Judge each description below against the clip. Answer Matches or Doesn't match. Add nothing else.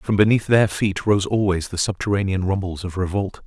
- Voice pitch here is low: Matches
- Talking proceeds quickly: Doesn't match